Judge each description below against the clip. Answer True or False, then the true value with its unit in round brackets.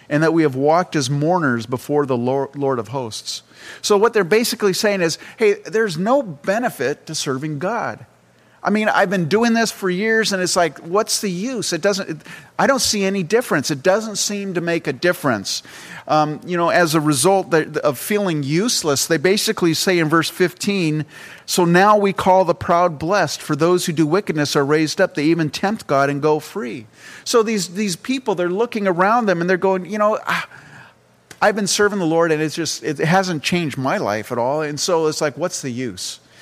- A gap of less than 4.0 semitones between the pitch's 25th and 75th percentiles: False (4.6 semitones)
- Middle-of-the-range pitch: True (175 Hz)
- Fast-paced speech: True (210 wpm)